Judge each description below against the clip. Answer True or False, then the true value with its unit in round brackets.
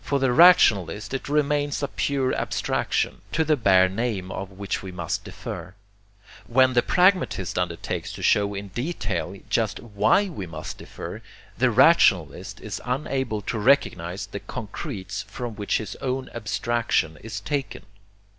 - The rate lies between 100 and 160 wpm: True (145 wpm)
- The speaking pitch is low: True (115 Hz)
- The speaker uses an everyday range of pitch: False (5.8 semitones)